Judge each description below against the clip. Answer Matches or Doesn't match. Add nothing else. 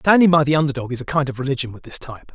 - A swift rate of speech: Matches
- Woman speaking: Doesn't match